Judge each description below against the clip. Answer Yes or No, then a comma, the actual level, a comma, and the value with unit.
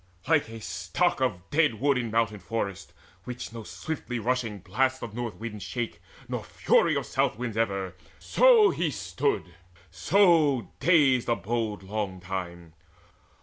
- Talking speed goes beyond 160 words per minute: No, average, 145 wpm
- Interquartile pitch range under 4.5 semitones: No, average, 4.9 semitones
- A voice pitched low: Yes, low, 115 Hz